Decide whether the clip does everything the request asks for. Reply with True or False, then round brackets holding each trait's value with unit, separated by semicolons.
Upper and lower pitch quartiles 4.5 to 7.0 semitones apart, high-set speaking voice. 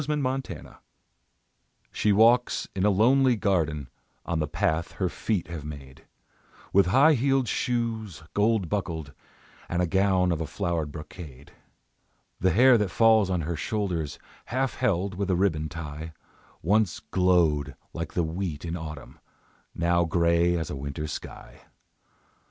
False (5.1 semitones; 90 Hz)